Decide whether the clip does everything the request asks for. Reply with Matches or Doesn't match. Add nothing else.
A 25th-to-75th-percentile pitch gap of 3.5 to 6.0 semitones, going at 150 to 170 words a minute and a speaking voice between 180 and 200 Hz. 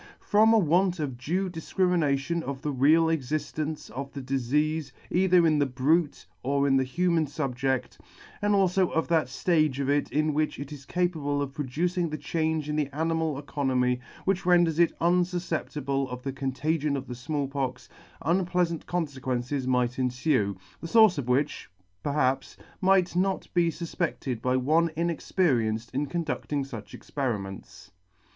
Doesn't match